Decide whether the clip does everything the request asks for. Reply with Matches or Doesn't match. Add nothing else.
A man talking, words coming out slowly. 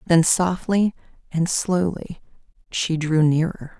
Doesn't match